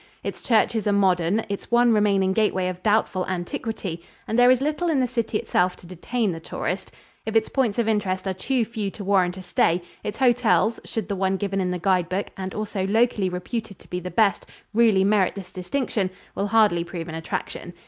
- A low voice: No, high, 200 Hz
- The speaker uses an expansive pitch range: No, average, 3.4 semitones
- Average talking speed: No, fast, 210 wpm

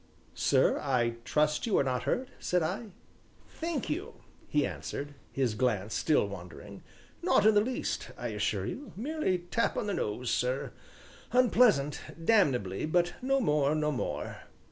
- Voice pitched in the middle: Yes, medium, 155 Hz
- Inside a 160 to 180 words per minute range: No, average, 145 wpm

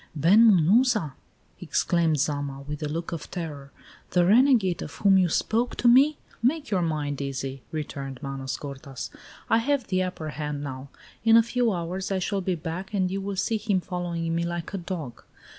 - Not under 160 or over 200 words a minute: Yes, average, 185 wpm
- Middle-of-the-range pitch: Yes, medium, 175 Hz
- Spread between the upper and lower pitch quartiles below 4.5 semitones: No, wide, 5.4 semitones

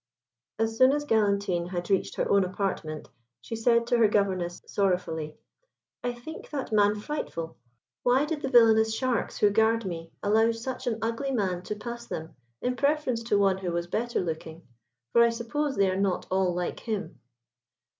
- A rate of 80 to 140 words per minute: No, average, 175 wpm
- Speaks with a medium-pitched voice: No, high, 215 Hz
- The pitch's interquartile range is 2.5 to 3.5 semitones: No, average, 4.3 semitones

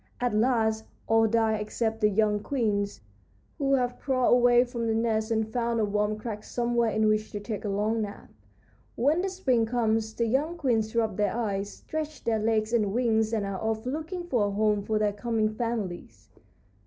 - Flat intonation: Yes, narrow, 2.2 semitones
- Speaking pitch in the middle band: No, high, 220 Hz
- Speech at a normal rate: Yes, average, 190 wpm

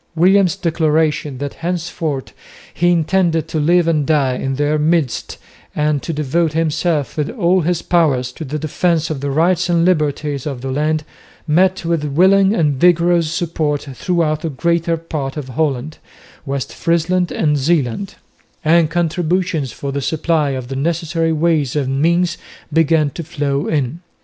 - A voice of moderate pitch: Yes, medium, 160 Hz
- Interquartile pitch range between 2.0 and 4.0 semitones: Yes, average, 2.8 semitones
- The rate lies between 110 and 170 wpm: Yes, average, 155 wpm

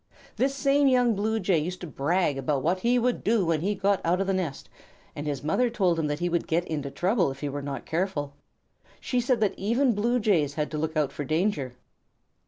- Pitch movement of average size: No, wide, 6.6 semitones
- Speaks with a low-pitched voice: No, medium, 180 Hz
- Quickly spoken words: Yes, fast, 230 wpm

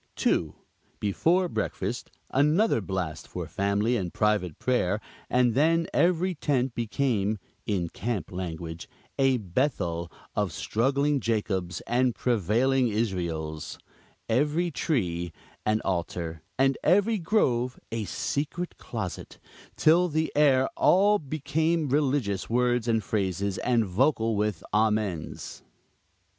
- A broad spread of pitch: Yes, wide, 6.9 semitones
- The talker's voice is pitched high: No, low, 115 Hz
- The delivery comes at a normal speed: No, slow, 110 wpm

